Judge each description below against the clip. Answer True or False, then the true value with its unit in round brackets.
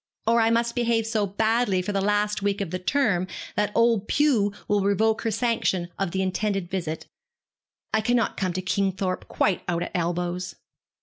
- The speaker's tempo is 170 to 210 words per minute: True (180 wpm)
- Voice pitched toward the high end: True (200 Hz)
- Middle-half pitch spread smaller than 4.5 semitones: True (3.4 semitones)